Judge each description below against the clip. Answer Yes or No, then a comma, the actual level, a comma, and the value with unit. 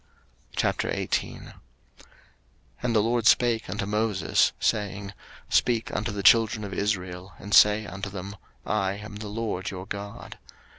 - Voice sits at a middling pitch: No, low, 105 Hz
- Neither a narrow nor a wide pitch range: No, narrow, 1.8 semitones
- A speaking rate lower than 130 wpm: No, average, 140 wpm